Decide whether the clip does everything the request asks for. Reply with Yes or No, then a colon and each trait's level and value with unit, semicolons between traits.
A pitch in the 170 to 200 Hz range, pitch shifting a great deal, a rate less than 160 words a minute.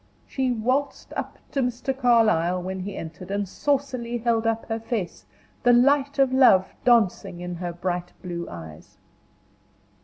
No: high, 225 Hz; wide, 6.0 semitones; average, 150 wpm